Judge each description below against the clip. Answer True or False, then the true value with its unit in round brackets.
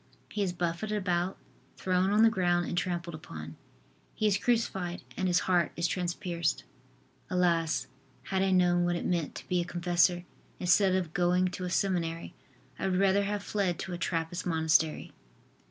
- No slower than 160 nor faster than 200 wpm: True (170 wpm)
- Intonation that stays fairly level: True (1.7 semitones)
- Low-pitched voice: False (180 Hz)